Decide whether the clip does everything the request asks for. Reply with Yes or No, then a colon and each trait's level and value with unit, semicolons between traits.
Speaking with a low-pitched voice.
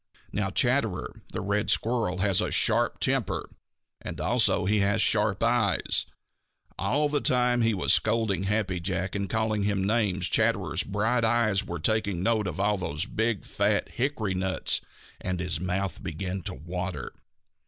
Yes: low, 100 Hz